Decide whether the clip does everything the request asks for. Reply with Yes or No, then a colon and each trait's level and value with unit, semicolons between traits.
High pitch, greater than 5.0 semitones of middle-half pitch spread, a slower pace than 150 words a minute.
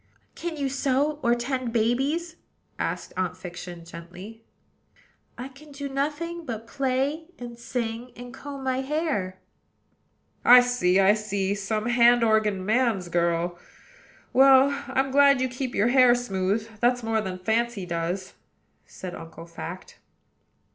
Yes: high, 235 Hz; wide, 5.6 semitones; slow, 135 wpm